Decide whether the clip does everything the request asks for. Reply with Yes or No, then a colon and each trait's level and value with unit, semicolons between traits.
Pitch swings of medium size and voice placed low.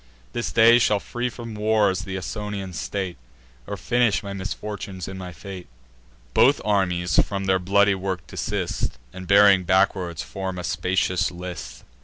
No: narrow, 2.1 semitones; very low, 95 Hz